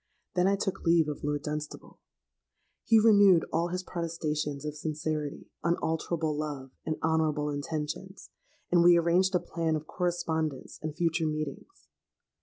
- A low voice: No, medium, 160 Hz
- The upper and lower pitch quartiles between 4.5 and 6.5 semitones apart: No, narrow, 2.5 semitones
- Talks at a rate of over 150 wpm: No, average, 140 wpm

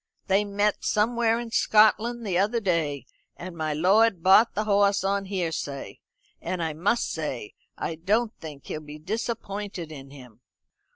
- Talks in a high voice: Yes, high, 195 Hz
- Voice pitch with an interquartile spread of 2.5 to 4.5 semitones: No, average, 5.0 semitones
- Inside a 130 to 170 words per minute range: Yes, average, 155 wpm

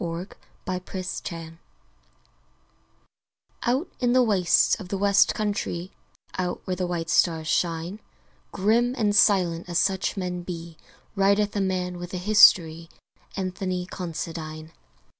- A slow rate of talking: Yes, slow, 120 wpm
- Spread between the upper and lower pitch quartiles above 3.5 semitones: No, average, 2.9 semitones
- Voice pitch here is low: No, medium, 180 Hz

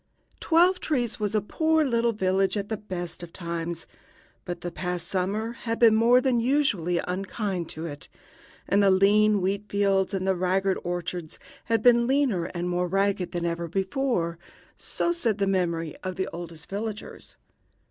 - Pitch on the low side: No, high, 195 Hz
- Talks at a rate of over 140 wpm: Yes, average, 170 wpm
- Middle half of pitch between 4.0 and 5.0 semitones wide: Yes, average, 4.3 semitones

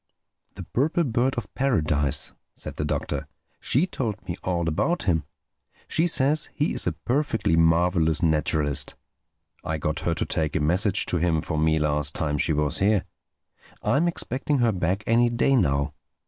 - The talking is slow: No, average, 165 wpm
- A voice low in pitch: Yes, very low, 90 Hz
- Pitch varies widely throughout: Yes, wide, 7.9 semitones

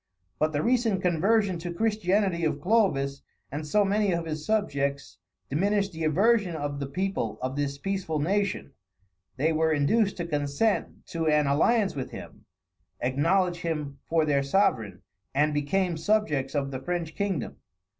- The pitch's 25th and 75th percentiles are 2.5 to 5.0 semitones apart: No, wide, 5.4 semitones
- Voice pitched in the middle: Yes, medium, 160 Hz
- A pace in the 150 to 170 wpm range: Yes, average, 155 wpm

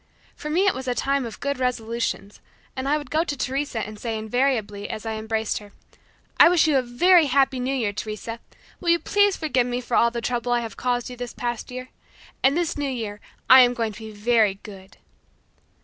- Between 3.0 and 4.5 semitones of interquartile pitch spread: Yes, average, 3.7 semitones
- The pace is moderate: No, fast, 220 wpm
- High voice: Yes, high, 245 Hz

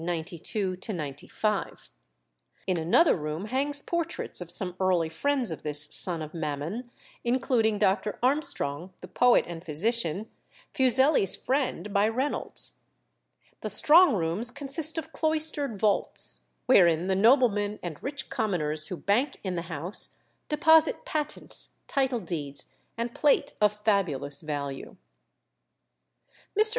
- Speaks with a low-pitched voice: No, high, 205 Hz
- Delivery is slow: Yes, slow, 120 wpm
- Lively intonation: Yes, wide, 7.9 semitones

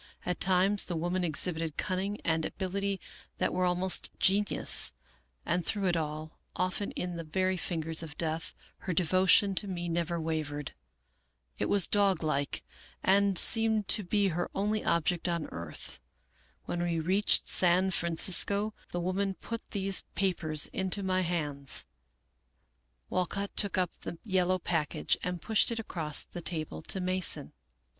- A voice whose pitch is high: No, medium, 180 Hz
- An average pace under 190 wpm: Yes, average, 150 wpm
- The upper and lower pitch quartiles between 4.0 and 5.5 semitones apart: No, average, 2.8 semitones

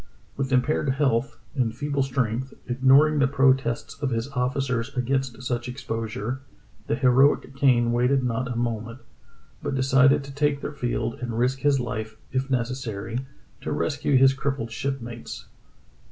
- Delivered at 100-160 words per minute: Yes, average, 150 wpm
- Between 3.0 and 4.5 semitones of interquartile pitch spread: No, narrow, 2.5 semitones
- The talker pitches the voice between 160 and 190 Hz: No, low, 130 Hz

